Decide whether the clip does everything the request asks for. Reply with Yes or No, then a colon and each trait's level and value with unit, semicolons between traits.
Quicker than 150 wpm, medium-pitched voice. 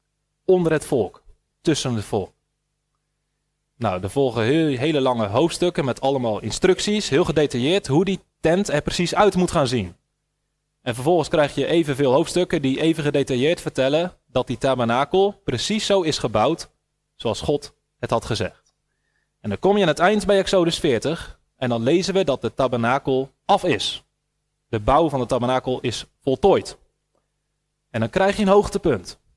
Yes: average, 165 wpm; medium, 145 Hz